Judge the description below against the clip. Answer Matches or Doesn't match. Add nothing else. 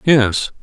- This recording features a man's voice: Matches